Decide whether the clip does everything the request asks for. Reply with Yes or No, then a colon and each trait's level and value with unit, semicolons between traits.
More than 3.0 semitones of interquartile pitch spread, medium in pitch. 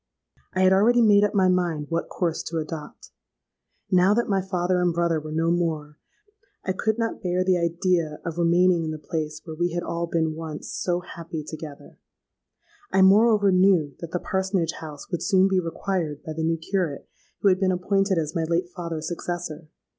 No: narrow, 2.6 semitones; medium, 175 Hz